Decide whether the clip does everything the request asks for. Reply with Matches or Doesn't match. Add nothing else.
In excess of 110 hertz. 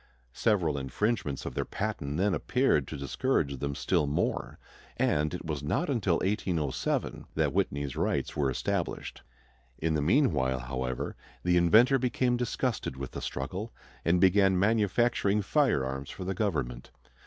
Doesn't match